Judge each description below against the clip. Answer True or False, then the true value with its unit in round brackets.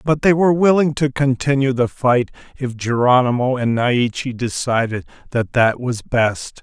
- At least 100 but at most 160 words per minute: True (155 wpm)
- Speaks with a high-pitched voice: False (125 Hz)